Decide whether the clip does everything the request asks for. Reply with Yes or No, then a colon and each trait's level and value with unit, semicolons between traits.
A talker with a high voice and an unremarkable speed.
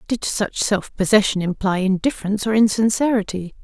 No: high, 205 Hz; slow, 130 wpm